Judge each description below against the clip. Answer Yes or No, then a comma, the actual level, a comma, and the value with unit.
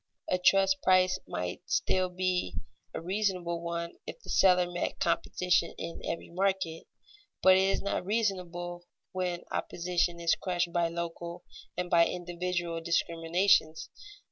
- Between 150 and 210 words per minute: No, slow, 135 wpm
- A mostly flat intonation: Yes, narrow, 1.5 semitones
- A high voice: No, medium, 175 Hz